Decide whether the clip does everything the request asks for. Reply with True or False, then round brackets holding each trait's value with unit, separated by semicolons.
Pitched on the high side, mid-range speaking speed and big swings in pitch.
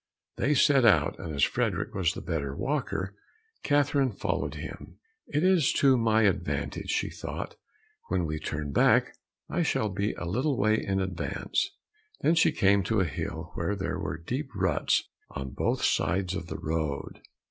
False (95 Hz; 170 wpm; 7.0 semitones)